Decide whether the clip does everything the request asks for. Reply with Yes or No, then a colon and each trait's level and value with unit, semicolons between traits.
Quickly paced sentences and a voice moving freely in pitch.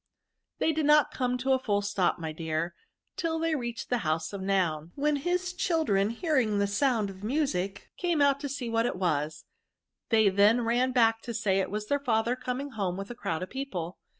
Yes: fast, 210 wpm; wide, 6.1 semitones